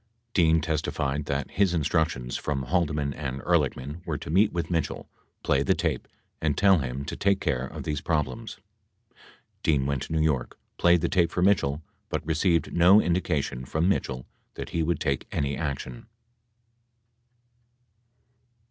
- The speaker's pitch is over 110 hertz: No, very low, 75 Hz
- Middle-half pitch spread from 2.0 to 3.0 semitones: No, average, 3.7 semitones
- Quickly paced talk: No, average, 160 wpm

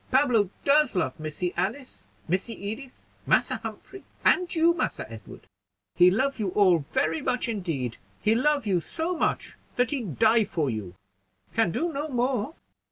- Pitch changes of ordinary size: No, wide, 7.6 semitones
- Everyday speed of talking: Yes, average, 160 wpm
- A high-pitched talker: Yes, high, 225 Hz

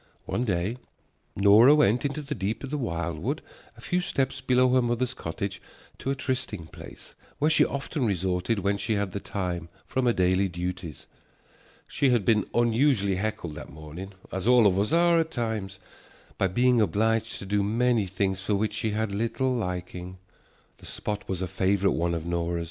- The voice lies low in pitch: Yes, low, 105 Hz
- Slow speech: No, average, 185 wpm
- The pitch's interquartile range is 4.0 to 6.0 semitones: Yes, average, 5.2 semitones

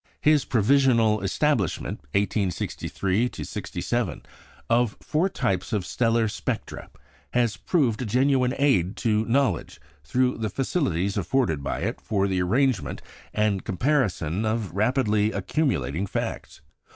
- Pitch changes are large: No, average, 4.9 semitones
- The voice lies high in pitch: No, low, 110 Hz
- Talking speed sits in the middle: No, slow, 115 wpm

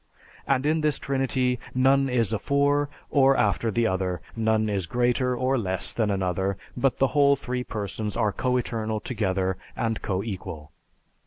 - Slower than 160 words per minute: Yes, average, 150 wpm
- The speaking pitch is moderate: No, low, 115 Hz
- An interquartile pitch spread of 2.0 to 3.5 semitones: No, average, 4.8 semitones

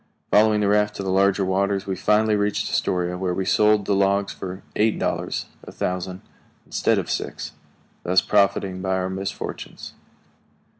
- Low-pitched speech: Yes, low, 100 Hz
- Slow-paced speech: No, average, 160 wpm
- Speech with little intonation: Yes, narrow, 1.7 semitones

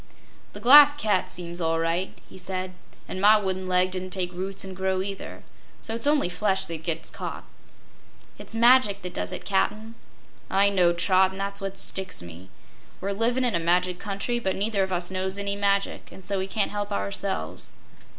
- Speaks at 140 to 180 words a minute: No, average, 190 wpm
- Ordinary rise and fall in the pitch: No, narrow, 1.9 semitones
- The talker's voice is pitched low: No, high, 190 Hz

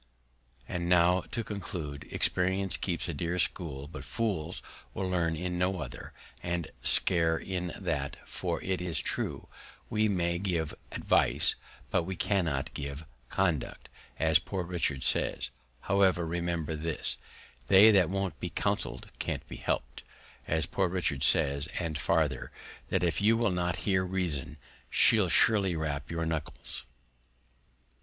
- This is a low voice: Yes, very low, 85 Hz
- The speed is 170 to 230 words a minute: No, average, 140 wpm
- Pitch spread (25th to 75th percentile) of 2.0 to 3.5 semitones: Yes, average, 2.9 semitones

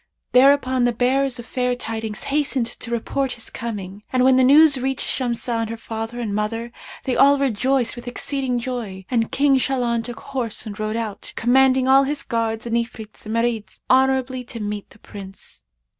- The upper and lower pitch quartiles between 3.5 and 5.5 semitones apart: No, average, 2.8 semitones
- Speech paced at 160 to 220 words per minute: Yes, average, 185 wpm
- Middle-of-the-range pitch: No, high, 240 Hz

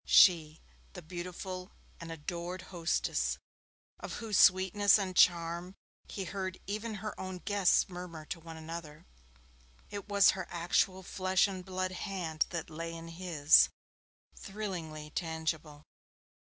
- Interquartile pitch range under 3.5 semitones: Yes, narrow, 2.4 semitones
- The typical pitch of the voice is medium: Yes, medium, 180 Hz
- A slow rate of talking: Yes, slow, 125 wpm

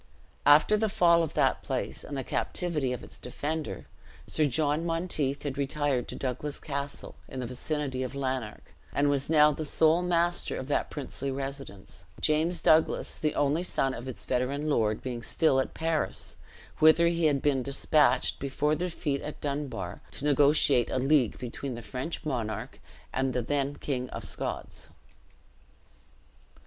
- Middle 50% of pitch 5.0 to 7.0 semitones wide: No, average, 3.0 semitones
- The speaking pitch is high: No, medium, 145 Hz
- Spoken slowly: No, average, 160 wpm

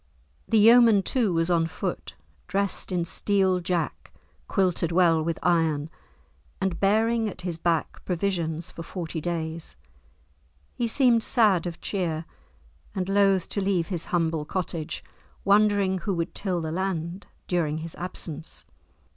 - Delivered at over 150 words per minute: No, average, 140 wpm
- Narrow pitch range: No, average, 3.2 semitones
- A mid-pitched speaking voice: Yes, medium, 180 Hz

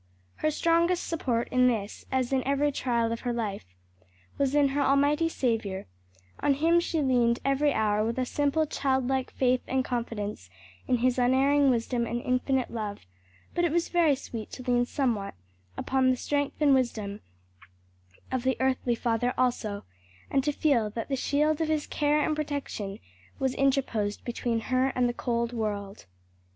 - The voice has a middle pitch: No, very high, 255 Hz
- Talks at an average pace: Yes, average, 165 wpm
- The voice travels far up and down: No, average, 3.4 semitones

